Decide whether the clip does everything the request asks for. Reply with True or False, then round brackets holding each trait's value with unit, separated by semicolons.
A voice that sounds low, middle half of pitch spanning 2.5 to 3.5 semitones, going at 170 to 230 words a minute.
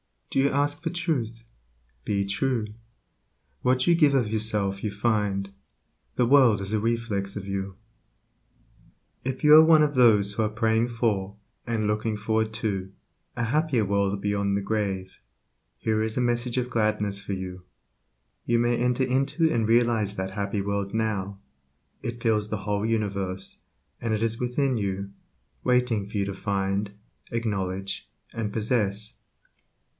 False (110 Hz; 3.2 semitones; 155 wpm)